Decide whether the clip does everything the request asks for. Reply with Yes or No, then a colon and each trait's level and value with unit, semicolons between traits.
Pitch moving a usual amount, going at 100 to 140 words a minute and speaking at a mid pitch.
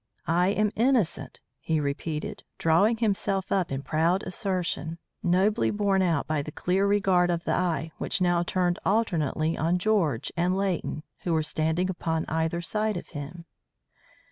No: average, 3.4 semitones; average, 155 wpm; medium, 175 Hz